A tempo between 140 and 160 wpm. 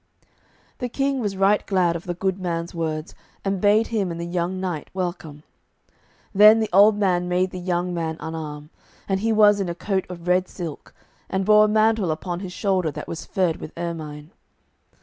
No: average, 190 wpm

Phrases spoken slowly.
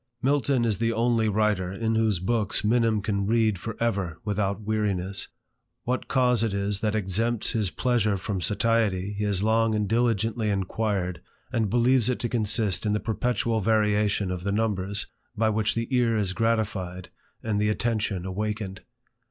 No: average, 165 wpm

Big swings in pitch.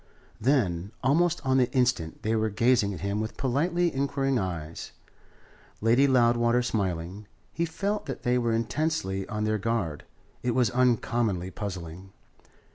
No: average, 4.9 semitones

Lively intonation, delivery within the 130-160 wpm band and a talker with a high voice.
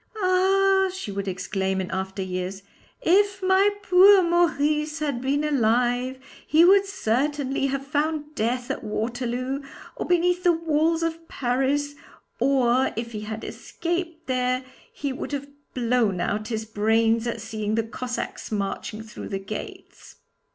Yes: wide, 6.7 semitones; average, 145 wpm; very high, 260 Hz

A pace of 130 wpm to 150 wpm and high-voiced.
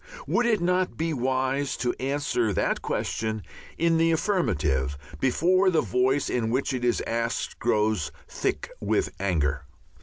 No: average, 145 wpm; low, 130 Hz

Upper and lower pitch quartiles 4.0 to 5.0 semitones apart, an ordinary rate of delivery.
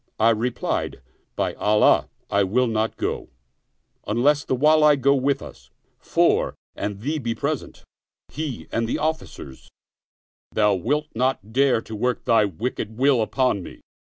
Yes: average, 4.5 semitones; average, 150 wpm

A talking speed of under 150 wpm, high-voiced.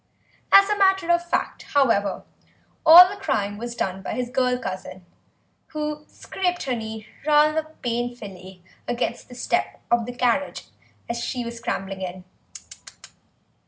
Yes: average, 140 wpm; high, 245 Hz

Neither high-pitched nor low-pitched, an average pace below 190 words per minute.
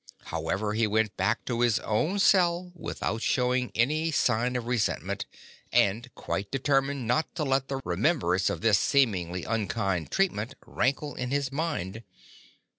No: low, 125 Hz; average, 155 wpm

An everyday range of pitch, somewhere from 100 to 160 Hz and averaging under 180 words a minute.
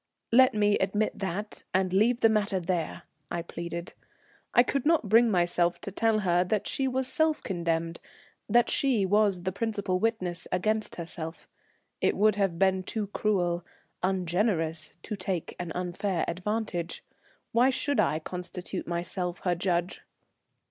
No: average, 3.7 semitones; high, 190 Hz; average, 150 wpm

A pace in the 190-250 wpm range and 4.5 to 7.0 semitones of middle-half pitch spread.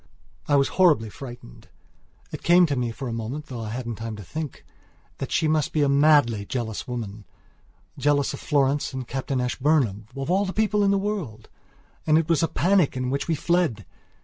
Yes: average, 195 wpm; average, 5.3 semitones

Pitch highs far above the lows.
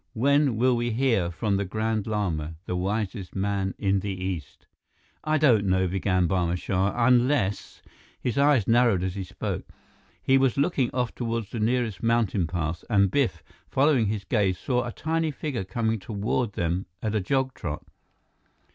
No: average, 4.7 semitones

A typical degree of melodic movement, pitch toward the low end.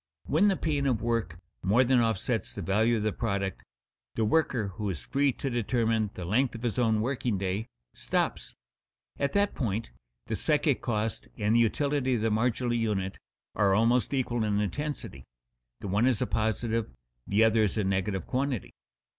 Yes: average, 3.3 semitones; low, 115 Hz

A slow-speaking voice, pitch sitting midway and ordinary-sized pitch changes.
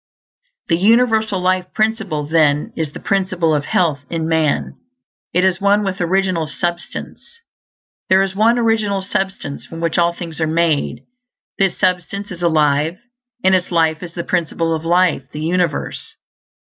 No: average, 160 wpm; medium, 175 Hz; average, 3.1 semitones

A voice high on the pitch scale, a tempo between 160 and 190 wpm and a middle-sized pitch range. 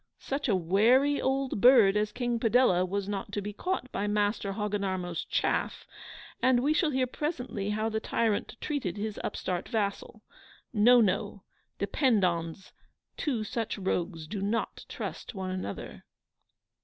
No: high, 210 Hz; average, 145 wpm; average, 4.1 semitones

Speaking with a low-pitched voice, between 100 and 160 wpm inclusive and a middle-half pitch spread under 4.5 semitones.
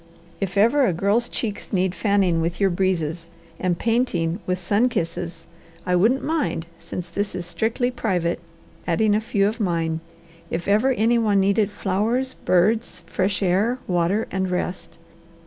No: high, 195 Hz; average, 155 wpm; average, 3.9 semitones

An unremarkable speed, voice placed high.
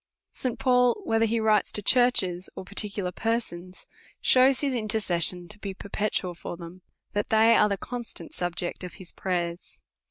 Yes: average, 170 wpm; high, 205 Hz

